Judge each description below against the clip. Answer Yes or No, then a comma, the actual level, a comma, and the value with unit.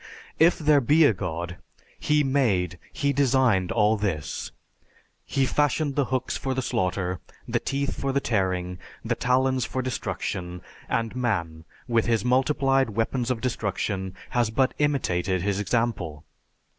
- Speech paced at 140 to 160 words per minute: Yes, average, 145 wpm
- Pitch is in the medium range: No, low, 115 Hz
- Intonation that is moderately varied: No, wide, 6.2 semitones